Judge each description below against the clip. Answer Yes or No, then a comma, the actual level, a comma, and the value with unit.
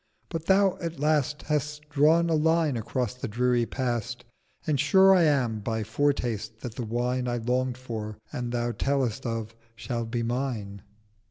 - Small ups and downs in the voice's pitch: No, average, 4.2 semitones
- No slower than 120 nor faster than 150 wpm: No, average, 165 wpm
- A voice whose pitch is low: Yes, low, 125 Hz